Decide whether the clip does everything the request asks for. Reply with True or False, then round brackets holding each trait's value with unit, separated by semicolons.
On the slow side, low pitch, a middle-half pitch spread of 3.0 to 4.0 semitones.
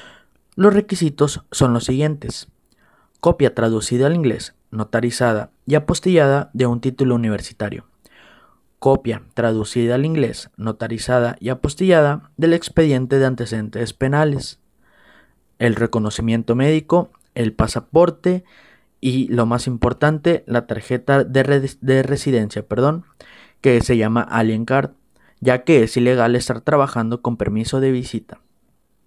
True (120 wpm; 125 Hz; 3.6 semitones)